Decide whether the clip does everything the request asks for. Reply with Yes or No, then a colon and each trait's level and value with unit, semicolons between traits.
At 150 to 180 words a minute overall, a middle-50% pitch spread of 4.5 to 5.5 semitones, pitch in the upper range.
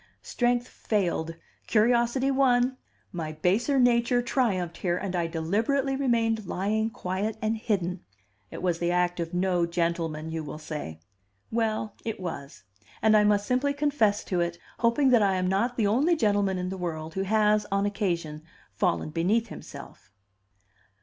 Yes: average, 155 wpm; average, 5.2 semitones; high, 200 Hz